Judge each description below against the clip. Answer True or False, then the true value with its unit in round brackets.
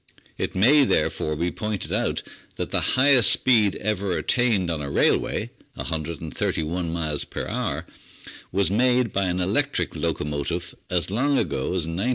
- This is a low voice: True (95 Hz)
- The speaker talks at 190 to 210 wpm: False (150 wpm)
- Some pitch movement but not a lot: False (6.1 semitones)